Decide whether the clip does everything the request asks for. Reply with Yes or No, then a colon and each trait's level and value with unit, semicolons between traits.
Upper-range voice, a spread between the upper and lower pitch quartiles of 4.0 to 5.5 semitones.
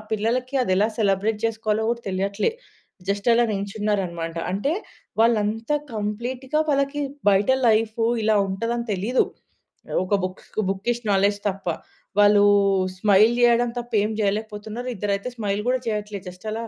No: high, 215 Hz; average, 2.8 semitones